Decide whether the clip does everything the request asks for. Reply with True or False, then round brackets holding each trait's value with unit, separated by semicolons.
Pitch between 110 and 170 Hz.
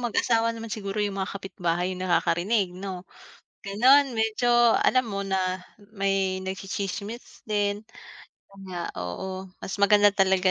False (195 Hz)